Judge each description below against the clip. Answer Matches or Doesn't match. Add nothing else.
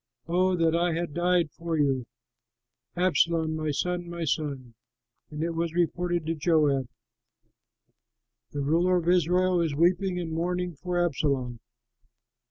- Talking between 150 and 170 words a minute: Doesn't match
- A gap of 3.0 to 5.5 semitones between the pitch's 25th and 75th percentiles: Doesn't match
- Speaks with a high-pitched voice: Doesn't match